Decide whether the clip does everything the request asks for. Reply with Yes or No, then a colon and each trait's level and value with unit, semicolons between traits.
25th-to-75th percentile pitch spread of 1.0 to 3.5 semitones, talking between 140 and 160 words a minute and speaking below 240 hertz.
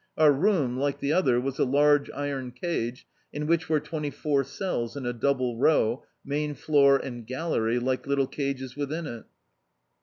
No: average, 2.8 semitones; average, 175 wpm; medium, 140 Hz